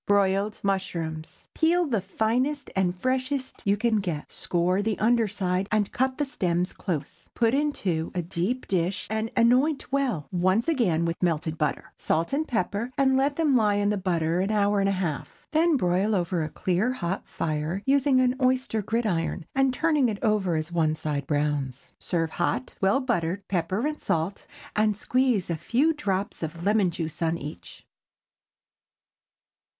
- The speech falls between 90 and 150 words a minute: No, average, 170 wpm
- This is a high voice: Yes, high, 200 Hz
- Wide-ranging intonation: Yes, wide, 6.6 semitones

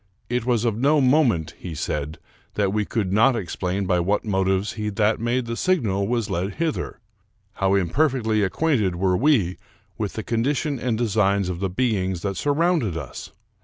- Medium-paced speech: Yes, average, 170 wpm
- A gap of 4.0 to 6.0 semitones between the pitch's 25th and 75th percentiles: Yes, average, 4.5 semitones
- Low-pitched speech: Yes, low, 105 Hz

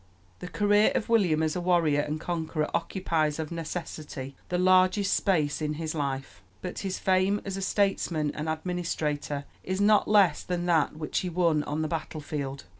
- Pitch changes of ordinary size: Yes, average, 3.5 semitones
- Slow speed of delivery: No, average, 180 wpm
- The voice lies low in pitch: No, medium, 165 Hz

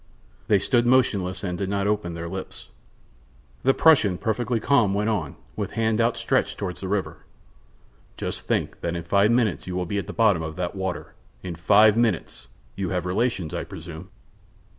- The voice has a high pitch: No, low, 100 Hz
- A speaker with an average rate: Yes, average, 180 wpm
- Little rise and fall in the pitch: No, average, 3.7 semitones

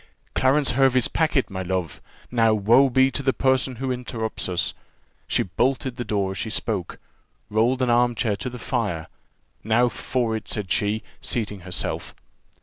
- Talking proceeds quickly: No, average, 165 wpm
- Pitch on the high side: No, low, 120 Hz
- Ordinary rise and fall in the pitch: Yes, average, 3.9 semitones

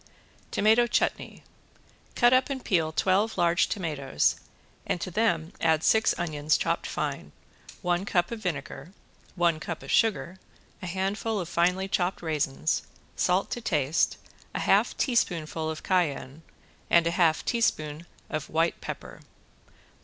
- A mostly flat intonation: No, average, 3.6 semitones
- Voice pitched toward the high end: No, medium, 175 Hz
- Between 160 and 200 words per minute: No, average, 140 wpm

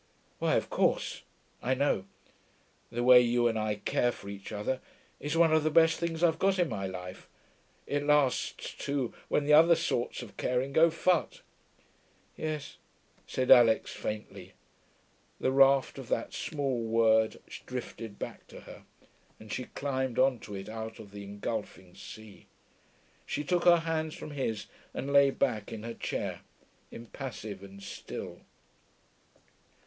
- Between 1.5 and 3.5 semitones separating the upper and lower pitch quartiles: No, average, 5.1 semitones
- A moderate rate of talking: Yes, average, 155 wpm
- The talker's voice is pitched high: No, low, 125 Hz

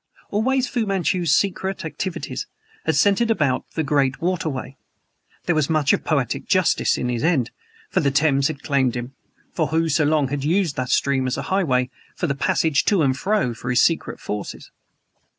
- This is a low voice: No, medium, 155 Hz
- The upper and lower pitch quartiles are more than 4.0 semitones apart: Yes, average, 5.1 semitones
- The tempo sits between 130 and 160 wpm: No, average, 180 wpm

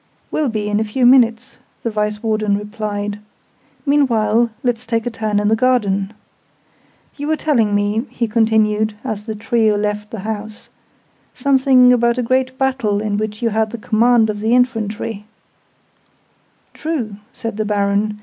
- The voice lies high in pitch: Yes, high, 220 Hz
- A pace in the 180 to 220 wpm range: No, average, 160 wpm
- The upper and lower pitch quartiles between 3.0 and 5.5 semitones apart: No, narrow, 2.6 semitones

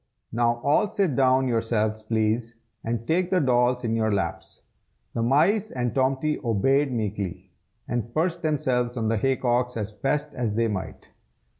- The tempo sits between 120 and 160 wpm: Yes, average, 155 wpm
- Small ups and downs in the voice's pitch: No, average, 3.3 semitones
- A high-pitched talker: No, low, 120 Hz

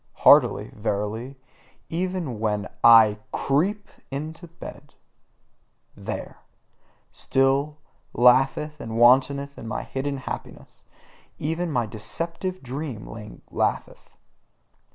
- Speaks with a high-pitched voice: No, low, 135 Hz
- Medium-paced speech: No, slow, 85 wpm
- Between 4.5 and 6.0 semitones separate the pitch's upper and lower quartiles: Yes, average, 5.3 semitones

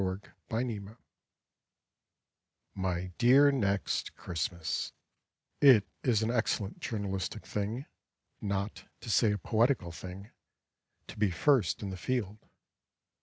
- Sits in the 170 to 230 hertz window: No, low, 105 Hz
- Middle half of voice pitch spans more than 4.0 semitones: No, average, 3.6 semitones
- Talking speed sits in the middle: No, slow, 115 wpm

